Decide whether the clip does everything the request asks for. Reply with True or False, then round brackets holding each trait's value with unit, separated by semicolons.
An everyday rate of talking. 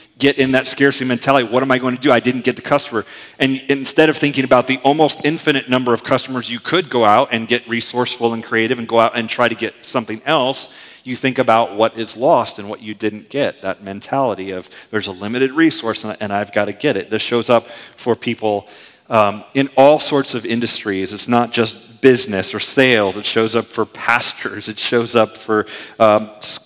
False (215 wpm)